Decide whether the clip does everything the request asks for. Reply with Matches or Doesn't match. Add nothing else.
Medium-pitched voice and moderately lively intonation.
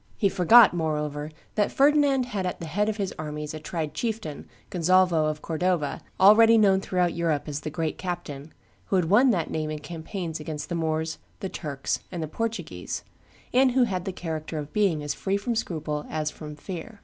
Matches